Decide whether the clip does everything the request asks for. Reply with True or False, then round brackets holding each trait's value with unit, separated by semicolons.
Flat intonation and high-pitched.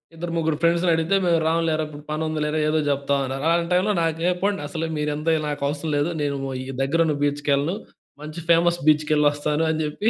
False (2.2 semitones; 155 Hz)